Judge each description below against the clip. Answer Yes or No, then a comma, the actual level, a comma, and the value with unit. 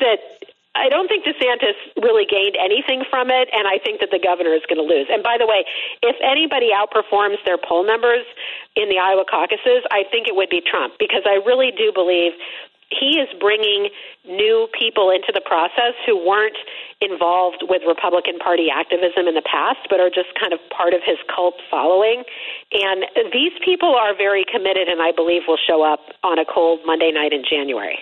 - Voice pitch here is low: No, high, 205 Hz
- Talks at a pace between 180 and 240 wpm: Yes, average, 195 wpm